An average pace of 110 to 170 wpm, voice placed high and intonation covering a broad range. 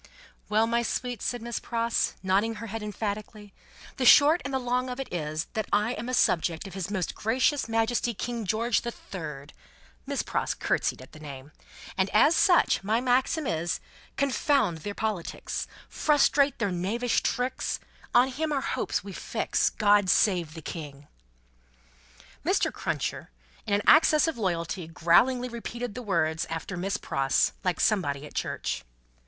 Yes: average, 160 wpm; high, 215 Hz; wide, 5.8 semitones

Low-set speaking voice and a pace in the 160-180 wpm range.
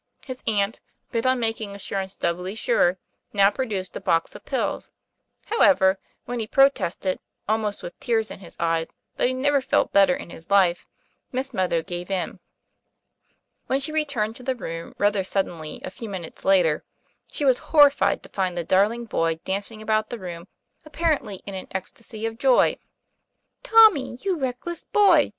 No: high, 215 Hz; average, 170 wpm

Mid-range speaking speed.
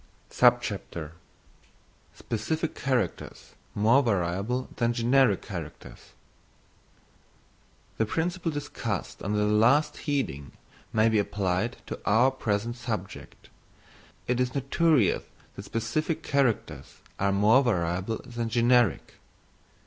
No: slow, 95 wpm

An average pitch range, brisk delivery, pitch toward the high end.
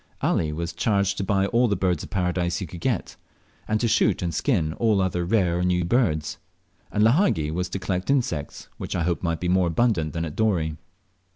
No: average, 3.9 semitones; fast, 210 wpm; very low, 90 Hz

